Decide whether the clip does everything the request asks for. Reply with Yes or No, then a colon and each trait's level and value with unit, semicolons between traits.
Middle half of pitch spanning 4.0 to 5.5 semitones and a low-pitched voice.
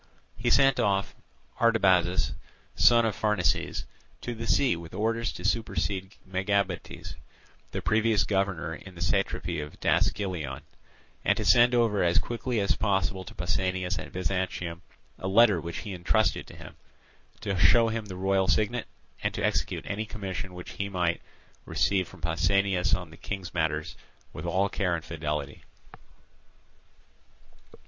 No: average, 3.4 semitones; very low, 95 Hz